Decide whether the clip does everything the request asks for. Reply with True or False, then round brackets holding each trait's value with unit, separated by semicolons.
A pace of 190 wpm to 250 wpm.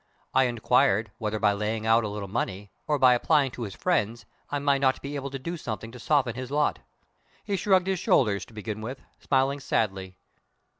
True (200 wpm)